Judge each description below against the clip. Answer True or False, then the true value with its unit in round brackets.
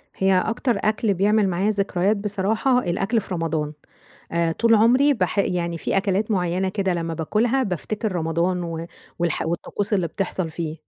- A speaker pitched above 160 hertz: True (190 Hz)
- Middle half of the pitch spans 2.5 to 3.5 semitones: False (3.9 semitones)